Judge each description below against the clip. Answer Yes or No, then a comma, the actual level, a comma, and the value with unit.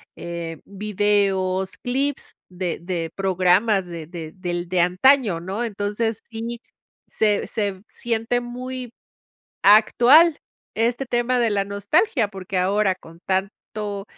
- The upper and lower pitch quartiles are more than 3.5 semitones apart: Yes, average, 4.1 semitones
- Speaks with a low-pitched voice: No, high, 205 Hz